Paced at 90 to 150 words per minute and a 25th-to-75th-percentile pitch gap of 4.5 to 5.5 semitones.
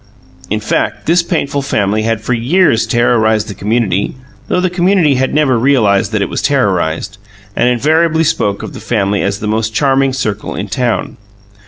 No: average, 175 wpm; average, 5.2 semitones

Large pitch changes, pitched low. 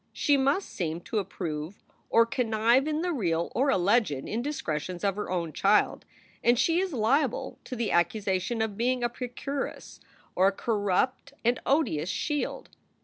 No: wide, 6.1 semitones; high, 225 Hz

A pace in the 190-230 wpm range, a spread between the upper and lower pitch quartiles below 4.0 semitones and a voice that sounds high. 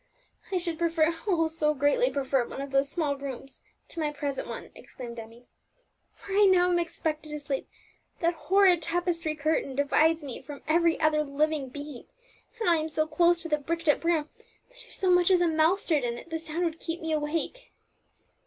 Yes: average, 200 wpm; average, 2.9 semitones; very high, 315 Hz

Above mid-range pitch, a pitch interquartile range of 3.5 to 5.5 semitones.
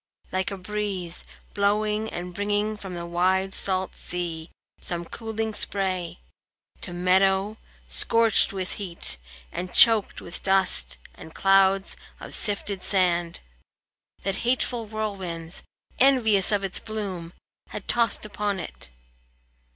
No: high, 195 Hz; average, 2.9 semitones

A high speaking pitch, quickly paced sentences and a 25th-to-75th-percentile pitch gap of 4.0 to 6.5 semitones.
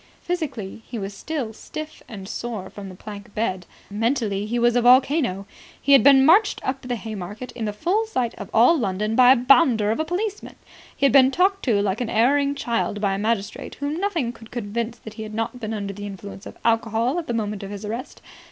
Yes: high, 230 Hz; fast, 220 wpm; average, 4.7 semitones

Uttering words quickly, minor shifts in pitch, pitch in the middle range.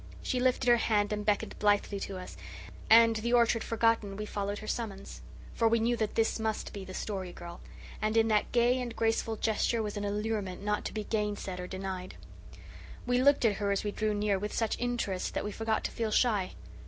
No: fast, 215 wpm; narrow, 2.1 semitones; high, 215 Hz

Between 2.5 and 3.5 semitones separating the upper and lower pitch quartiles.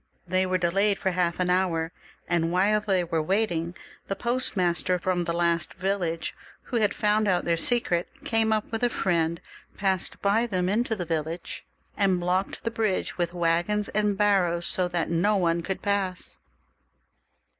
Yes: average, 3.2 semitones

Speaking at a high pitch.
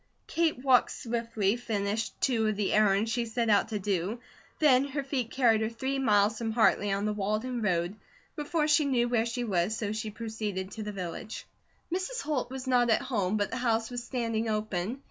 Yes: high, 225 Hz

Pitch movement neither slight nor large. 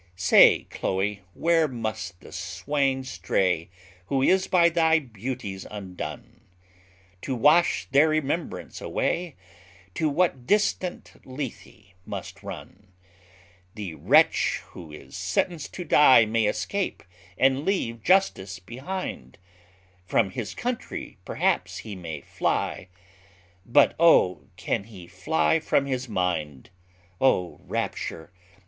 No: wide, 8.8 semitones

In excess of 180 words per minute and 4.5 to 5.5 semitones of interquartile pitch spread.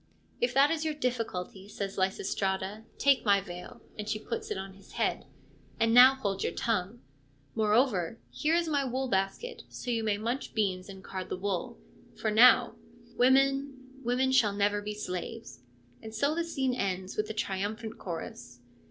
Yes: average, 195 wpm; average, 4.9 semitones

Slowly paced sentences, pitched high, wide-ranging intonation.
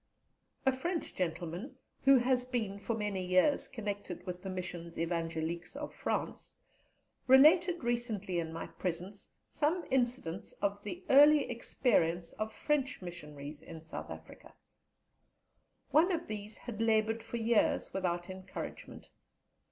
Yes: slow, 130 wpm; high, 210 Hz; wide, 6.6 semitones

